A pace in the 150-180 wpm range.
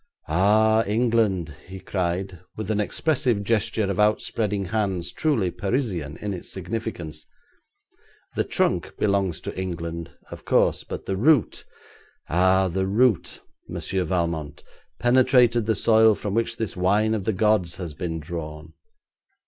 No: slow, 135 wpm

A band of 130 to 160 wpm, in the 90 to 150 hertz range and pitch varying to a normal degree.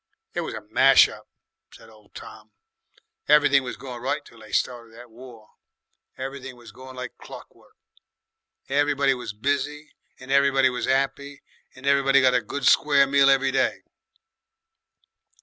No: average, 150 wpm; low, 135 Hz; narrow, 2.0 semitones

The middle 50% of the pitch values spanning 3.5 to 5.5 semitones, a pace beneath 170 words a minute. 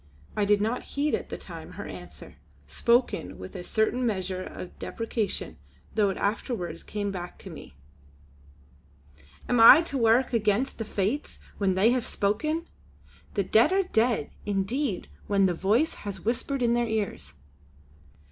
Yes: average, 4.0 semitones; average, 155 wpm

